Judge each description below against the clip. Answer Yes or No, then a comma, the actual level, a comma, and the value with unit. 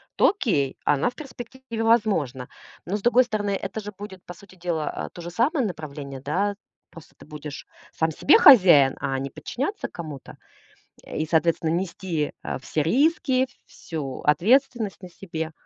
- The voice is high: No, medium, 180 Hz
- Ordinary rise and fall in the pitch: No, wide, 7.2 semitones